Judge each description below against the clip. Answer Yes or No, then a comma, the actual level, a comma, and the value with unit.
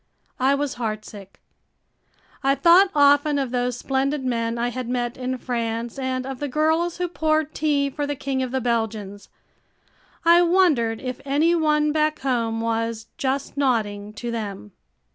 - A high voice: Yes, very high, 260 Hz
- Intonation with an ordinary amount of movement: Yes, average, 4.1 semitones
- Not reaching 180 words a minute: Yes, average, 160 wpm